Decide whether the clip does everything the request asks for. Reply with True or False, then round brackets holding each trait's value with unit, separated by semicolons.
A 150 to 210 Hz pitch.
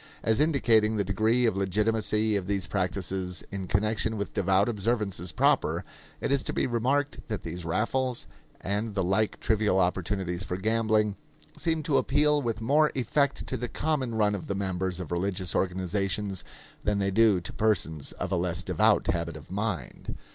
False (105 Hz)